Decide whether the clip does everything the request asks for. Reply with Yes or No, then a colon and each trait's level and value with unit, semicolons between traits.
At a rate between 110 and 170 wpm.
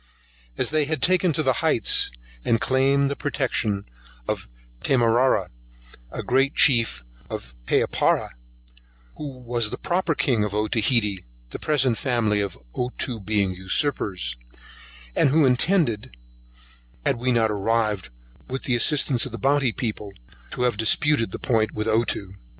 Yes: average, 140 wpm